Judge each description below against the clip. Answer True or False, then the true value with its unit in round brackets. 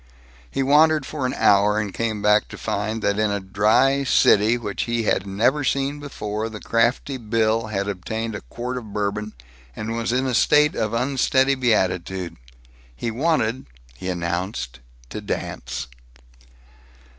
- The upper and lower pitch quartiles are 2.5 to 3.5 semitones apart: False (3.9 semitones)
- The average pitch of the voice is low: True (110 Hz)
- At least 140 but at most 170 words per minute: True (155 wpm)